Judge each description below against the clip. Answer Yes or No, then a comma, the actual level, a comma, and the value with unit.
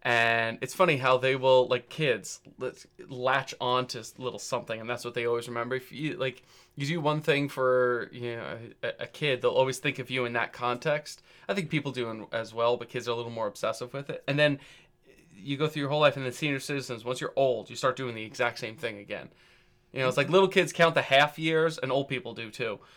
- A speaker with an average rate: No, fast, 245 wpm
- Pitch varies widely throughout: No, average, 3.3 semitones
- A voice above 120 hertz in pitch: Yes, low, 130 Hz